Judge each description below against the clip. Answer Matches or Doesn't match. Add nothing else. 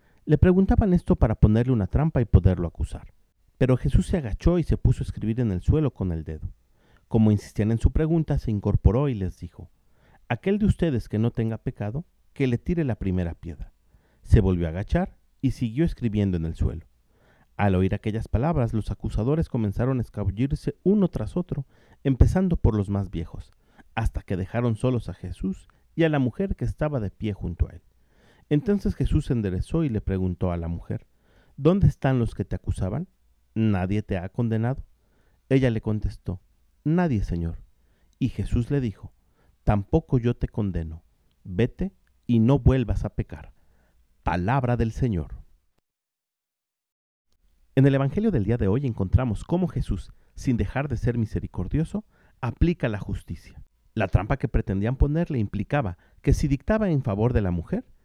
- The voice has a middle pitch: Doesn't match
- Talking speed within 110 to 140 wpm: Doesn't match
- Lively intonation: Matches